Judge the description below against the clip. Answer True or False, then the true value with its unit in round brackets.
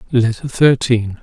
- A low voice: True (120 Hz)